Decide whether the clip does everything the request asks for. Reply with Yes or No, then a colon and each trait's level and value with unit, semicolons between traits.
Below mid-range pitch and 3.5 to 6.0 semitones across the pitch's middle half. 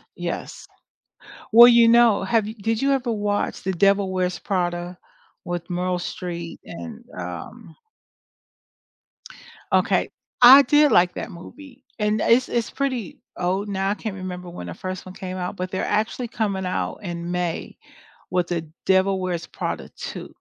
No: high, 190 Hz; average, 4.1 semitones